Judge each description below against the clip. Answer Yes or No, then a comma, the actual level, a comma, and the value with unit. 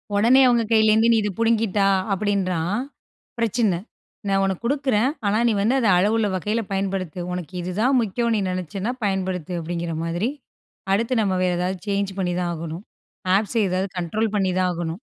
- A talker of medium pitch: No, high, 195 Hz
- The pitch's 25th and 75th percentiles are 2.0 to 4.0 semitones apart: Yes, average, 3.6 semitones